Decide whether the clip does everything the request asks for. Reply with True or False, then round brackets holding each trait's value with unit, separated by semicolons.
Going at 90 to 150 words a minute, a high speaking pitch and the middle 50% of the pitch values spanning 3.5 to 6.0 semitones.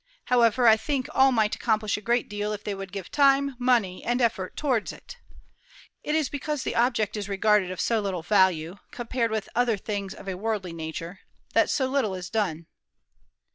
False (190 wpm; 215 Hz; 4.2 semitones)